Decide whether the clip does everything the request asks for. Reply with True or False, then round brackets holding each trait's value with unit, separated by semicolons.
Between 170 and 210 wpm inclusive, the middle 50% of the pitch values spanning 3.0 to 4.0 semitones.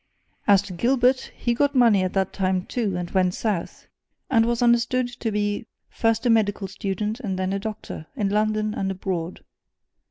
True (180 wpm; 3.4 semitones)